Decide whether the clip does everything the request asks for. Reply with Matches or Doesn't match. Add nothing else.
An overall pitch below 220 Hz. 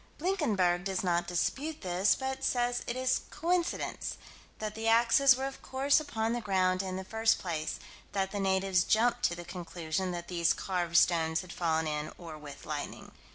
Matches